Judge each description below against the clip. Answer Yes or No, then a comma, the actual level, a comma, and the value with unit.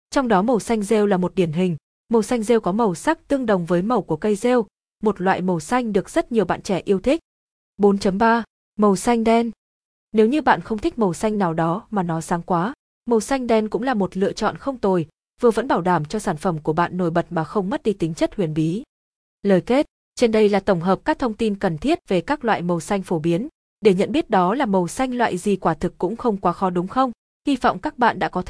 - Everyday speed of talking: No, fast, 255 wpm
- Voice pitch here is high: Yes, high, 205 Hz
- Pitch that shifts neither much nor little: Yes, average, 4.7 semitones